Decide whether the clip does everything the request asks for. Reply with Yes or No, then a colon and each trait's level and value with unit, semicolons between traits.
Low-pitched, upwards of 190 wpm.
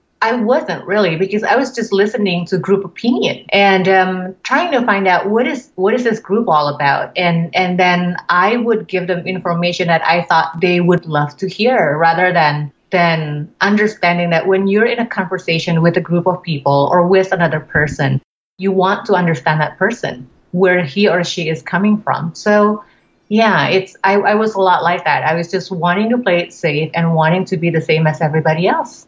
No: medium, 180 Hz; fast, 205 wpm